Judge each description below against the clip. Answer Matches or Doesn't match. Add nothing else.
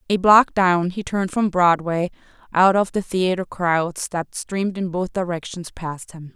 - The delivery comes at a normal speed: Matches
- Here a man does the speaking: Doesn't match